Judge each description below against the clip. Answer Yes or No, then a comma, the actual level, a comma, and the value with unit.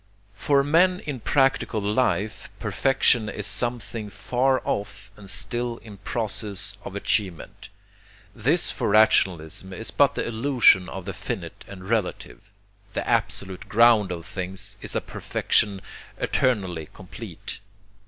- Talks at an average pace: No, slow, 125 wpm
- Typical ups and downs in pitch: Yes, average, 4.1 semitones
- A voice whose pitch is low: Yes, low, 105 Hz